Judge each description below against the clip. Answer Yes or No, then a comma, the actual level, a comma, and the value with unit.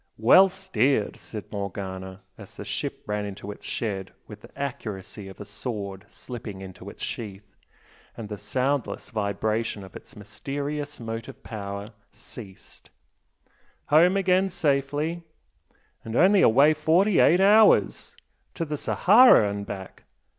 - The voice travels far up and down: Yes, wide, 6.5 semitones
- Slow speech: Yes, slow, 130 wpm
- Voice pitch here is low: Yes, low, 115 Hz